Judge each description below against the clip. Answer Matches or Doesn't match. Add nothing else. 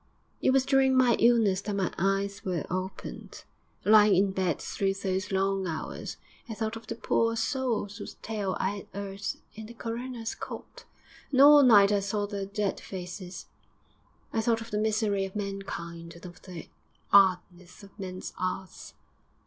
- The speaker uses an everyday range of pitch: Matches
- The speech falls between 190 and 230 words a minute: Doesn't match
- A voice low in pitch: Doesn't match